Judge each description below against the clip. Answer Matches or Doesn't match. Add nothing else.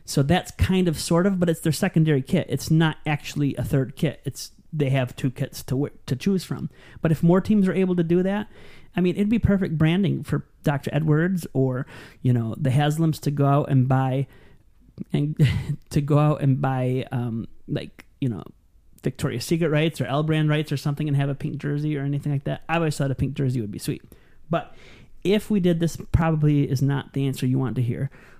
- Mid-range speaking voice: Matches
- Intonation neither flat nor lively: Matches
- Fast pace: Matches